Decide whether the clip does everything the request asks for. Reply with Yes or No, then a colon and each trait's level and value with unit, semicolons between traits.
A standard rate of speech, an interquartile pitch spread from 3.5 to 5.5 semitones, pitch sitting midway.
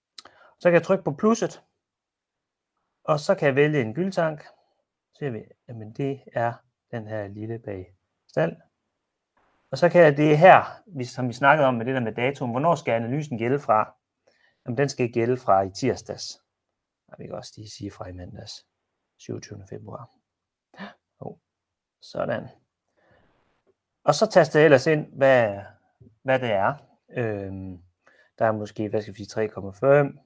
No: average, 160 wpm; average, 5.1 semitones; low, 125 Hz